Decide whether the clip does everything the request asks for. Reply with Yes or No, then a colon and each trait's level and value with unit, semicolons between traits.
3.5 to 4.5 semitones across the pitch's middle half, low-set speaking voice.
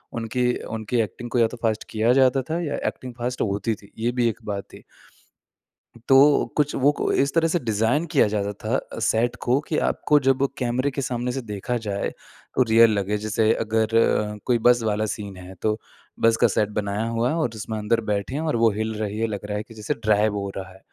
No: average, 2.9 semitones; low, 115 Hz